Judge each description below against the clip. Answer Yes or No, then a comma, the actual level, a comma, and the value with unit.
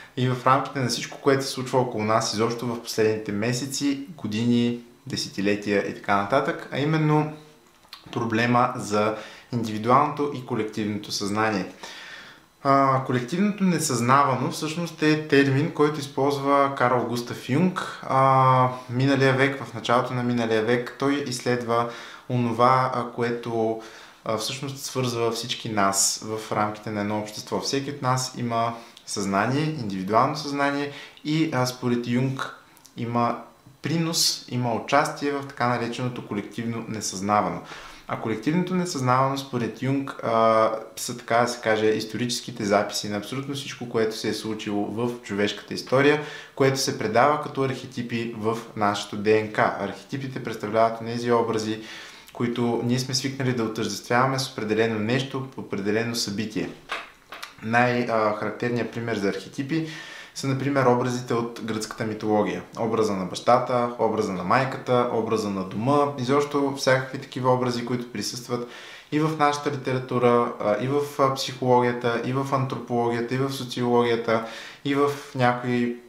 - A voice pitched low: Yes, low, 120 Hz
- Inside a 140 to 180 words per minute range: No, average, 130 wpm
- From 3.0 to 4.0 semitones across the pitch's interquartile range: Yes, average, 3.4 semitones